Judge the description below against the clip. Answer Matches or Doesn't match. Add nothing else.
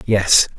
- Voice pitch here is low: Matches